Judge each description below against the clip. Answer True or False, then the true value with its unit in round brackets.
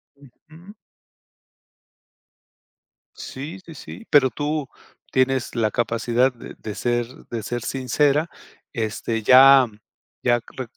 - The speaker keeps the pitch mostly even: False (3.3 semitones)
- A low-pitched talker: True (130 Hz)